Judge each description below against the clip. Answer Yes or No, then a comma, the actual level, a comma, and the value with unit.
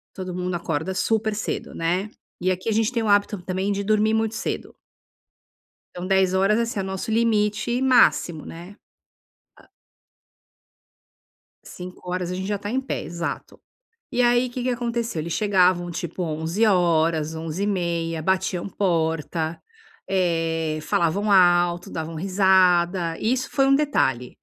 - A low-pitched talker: No, medium, 185 Hz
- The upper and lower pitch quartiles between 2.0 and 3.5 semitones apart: No, average, 3.9 semitones